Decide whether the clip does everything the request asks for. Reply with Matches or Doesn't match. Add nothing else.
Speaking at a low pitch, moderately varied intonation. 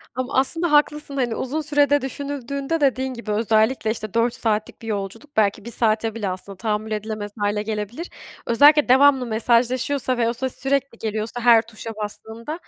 Doesn't match